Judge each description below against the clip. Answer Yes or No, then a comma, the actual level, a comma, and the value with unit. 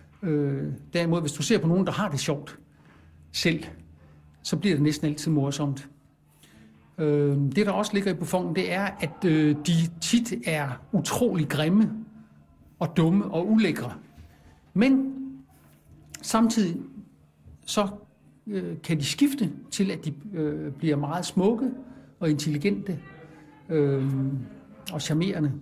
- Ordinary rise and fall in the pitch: No, wide, 5.8 semitones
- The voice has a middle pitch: Yes, medium, 155 Hz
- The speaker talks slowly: Yes, slow, 135 wpm